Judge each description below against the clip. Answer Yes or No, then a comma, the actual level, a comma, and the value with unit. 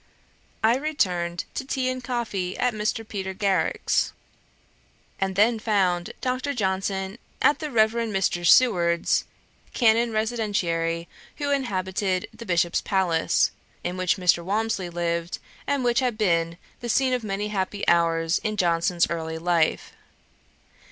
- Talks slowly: Yes, slow, 130 wpm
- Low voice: No, high, 195 Hz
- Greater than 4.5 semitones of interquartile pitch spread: Yes, average, 5.0 semitones